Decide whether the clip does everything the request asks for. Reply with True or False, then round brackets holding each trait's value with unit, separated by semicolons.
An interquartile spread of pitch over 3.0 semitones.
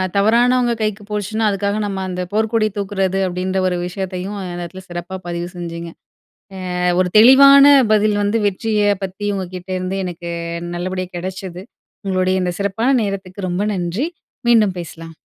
False (2.6 semitones)